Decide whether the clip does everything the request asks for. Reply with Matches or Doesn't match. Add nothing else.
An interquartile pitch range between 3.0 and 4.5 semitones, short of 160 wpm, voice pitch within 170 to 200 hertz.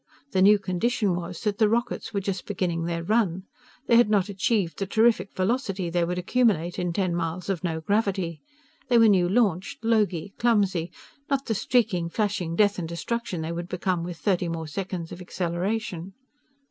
Doesn't match